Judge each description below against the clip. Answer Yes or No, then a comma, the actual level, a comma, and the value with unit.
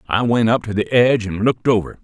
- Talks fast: Yes, fast, 265 wpm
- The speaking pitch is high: No, low, 110 Hz